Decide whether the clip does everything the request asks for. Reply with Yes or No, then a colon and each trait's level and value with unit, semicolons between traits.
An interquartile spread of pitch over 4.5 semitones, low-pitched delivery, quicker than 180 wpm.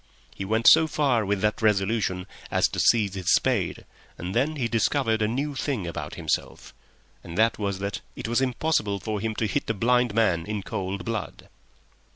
No: average, 3.3 semitones; low, 110 Hz; average, 190 wpm